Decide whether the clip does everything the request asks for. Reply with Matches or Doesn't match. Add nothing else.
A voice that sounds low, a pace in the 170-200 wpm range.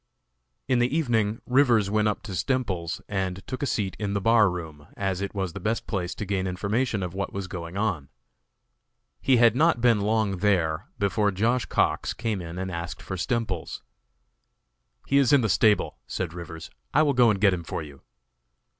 Matches